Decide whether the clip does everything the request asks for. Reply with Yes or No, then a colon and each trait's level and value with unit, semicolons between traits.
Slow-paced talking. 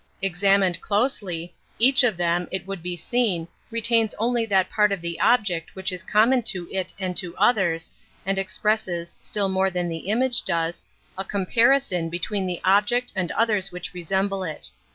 No: average, 175 wpm